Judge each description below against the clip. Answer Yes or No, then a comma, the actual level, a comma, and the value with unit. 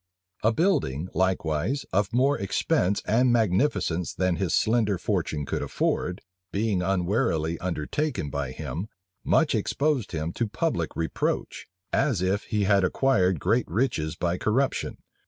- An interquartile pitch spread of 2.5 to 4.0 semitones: No, wide, 5.5 semitones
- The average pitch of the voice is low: Yes, very low, 95 Hz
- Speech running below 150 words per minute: Yes, slow, 135 wpm